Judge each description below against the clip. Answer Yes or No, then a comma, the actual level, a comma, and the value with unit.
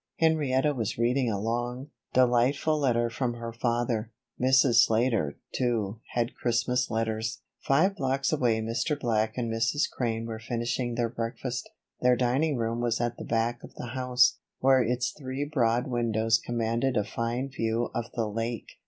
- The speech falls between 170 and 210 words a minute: No, average, 160 wpm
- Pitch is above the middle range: No, low, 120 Hz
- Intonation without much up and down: Yes, narrow, 2.1 semitones